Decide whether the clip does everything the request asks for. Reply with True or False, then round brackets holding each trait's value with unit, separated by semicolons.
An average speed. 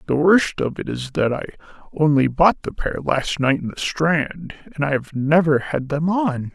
False (210 wpm)